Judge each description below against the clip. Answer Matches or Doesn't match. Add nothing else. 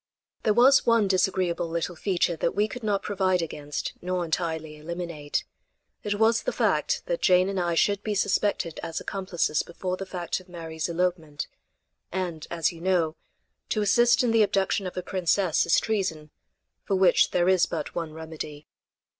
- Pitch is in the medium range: Matches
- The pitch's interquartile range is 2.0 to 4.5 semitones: Matches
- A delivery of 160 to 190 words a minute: Matches